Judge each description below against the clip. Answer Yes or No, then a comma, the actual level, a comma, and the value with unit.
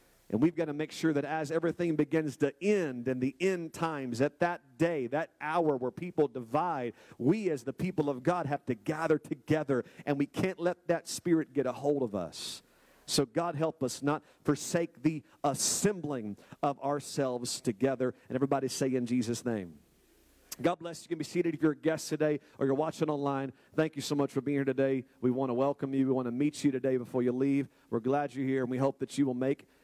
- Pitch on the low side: No, medium, 145 Hz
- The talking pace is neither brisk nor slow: No, fast, 225 wpm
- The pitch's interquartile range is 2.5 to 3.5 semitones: Yes, average, 3.2 semitones